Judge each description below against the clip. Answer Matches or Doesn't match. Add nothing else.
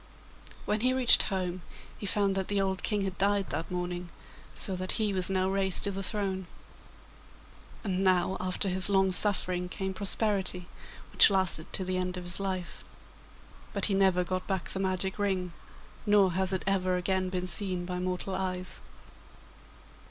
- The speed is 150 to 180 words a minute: Matches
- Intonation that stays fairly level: Matches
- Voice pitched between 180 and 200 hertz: Matches